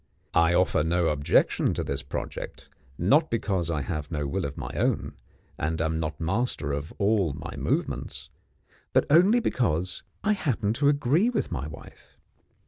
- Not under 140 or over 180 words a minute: Yes, average, 160 wpm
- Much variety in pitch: Yes, wide, 8.2 semitones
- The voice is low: Yes, very low, 90 Hz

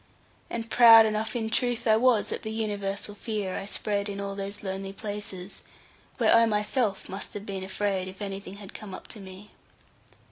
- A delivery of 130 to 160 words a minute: No, average, 185 wpm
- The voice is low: No, high, 205 Hz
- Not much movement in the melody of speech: Yes, narrow, 2.0 semitones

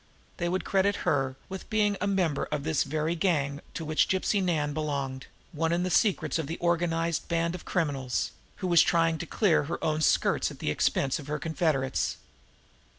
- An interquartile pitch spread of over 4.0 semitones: No, average, 3.0 semitones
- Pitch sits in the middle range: Yes, medium, 165 Hz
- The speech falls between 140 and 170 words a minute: No, average, 190 wpm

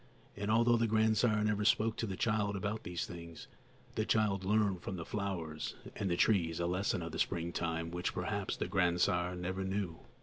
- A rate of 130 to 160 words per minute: No, average, 180 wpm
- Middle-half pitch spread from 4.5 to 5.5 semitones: No, average, 3.5 semitones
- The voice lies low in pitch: Yes, very low, 95 Hz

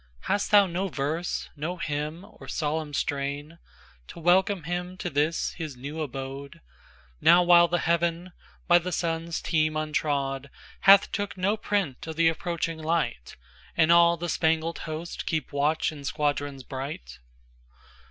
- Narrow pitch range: No, average, 3.4 semitones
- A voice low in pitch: No, medium, 160 Hz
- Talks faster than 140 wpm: No, slow, 135 wpm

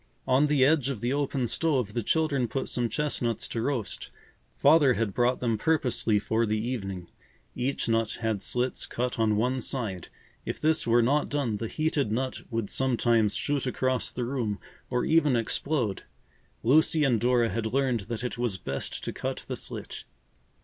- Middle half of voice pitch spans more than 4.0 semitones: No, average, 3.4 semitones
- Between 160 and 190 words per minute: Yes, average, 175 wpm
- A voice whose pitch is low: Yes, low, 125 Hz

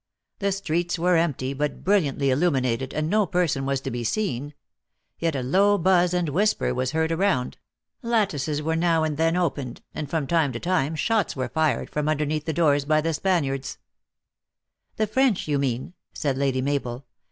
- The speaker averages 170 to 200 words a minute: Yes, average, 185 wpm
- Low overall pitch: No, medium, 155 Hz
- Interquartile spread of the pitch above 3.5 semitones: Yes, average, 4.4 semitones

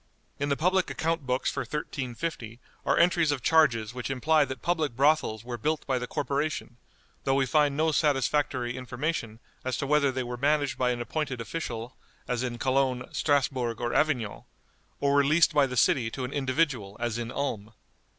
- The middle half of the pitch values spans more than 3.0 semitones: Yes, average, 3.7 semitones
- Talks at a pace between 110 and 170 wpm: No, average, 180 wpm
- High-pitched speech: No, low, 135 Hz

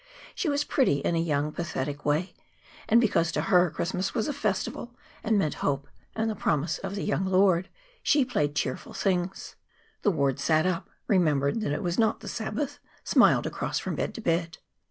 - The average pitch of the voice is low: No, medium, 180 Hz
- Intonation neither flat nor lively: No, wide, 6.0 semitones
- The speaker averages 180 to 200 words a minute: Yes, average, 190 wpm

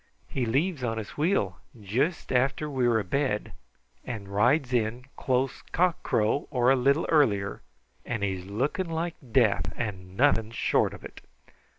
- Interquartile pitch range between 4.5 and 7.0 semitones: Yes, average, 5.1 semitones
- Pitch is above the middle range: No, low, 125 Hz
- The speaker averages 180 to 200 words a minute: No, average, 150 wpm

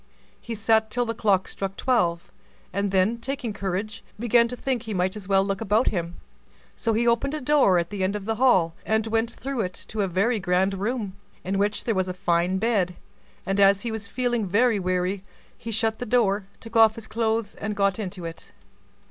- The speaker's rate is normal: No, fast, 210 wpm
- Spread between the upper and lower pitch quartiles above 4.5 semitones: No, average, 3.3 semitones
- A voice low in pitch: No, high, 210 Hz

